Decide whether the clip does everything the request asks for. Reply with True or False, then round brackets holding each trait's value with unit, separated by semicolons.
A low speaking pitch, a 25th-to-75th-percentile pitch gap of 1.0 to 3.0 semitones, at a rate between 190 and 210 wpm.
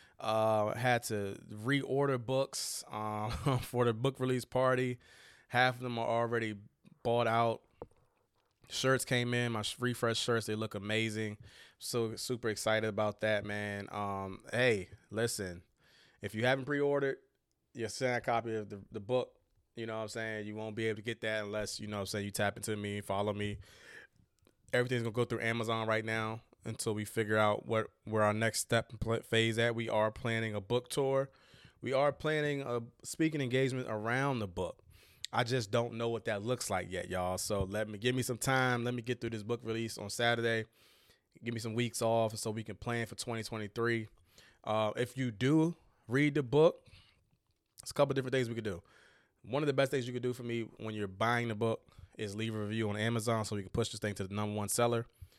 True (115 Hz; 2.6 semitones; 205 wpm)